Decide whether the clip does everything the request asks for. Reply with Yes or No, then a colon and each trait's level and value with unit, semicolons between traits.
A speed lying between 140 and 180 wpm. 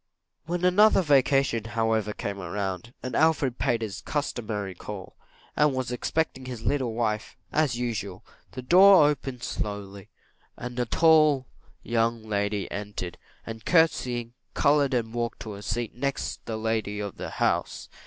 Yes: average, 145 wpm